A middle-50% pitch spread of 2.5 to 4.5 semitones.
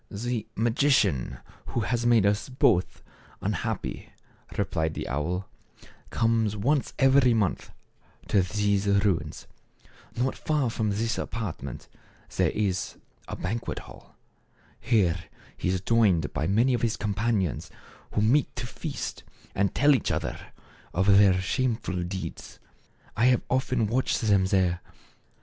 Yes: average, 4.1 semitones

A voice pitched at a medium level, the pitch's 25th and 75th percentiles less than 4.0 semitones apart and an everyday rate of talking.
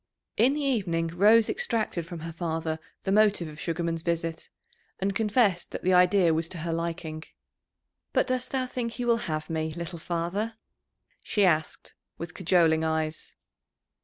No: medium, 170 Hz; average, 4.6 semitones; average, 160 wpm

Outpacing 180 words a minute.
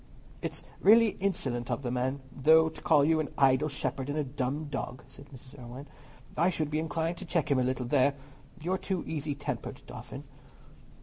Yes: average, 200 wpm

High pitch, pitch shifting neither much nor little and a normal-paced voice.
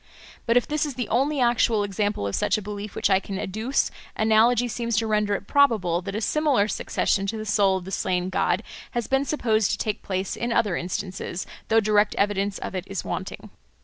No: high, 210 Hz; average, 3.2 semitones; fast, 210 wpm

